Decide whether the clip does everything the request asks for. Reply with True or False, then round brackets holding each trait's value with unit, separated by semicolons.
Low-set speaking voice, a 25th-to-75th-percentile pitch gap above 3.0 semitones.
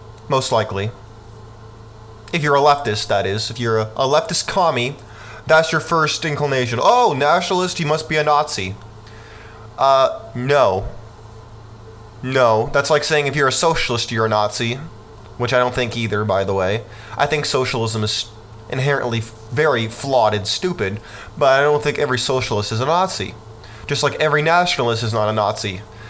True (115 Hz; 4.6 semitones)